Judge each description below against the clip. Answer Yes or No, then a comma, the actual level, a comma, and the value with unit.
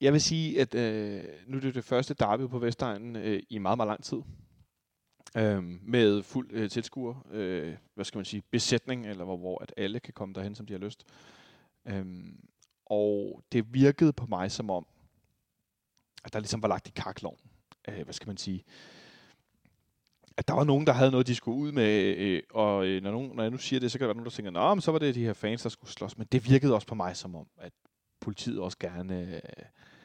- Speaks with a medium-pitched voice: No, low, 110 Hz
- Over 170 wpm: Yes, average, 220 wpm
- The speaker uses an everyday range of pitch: Yes, average, 4.2 semitones